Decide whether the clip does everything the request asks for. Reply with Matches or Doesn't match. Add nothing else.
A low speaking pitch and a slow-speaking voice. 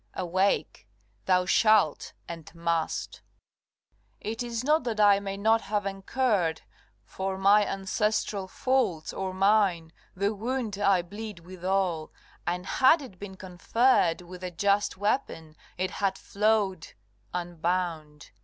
Doesn't match